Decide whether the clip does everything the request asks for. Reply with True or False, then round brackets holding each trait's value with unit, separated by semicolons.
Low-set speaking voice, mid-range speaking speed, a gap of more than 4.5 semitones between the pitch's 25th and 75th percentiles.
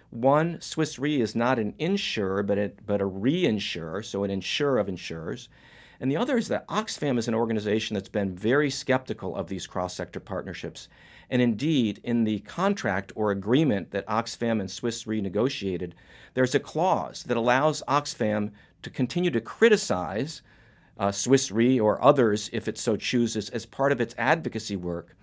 True (115 Hz; 165 wpm; 5.1 semitones)